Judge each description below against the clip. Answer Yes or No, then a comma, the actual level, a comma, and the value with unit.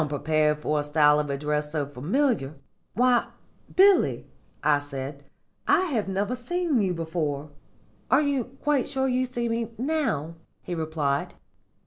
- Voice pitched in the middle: Yes, medium, 165 Hz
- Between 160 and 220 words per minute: No, average, 140 wpm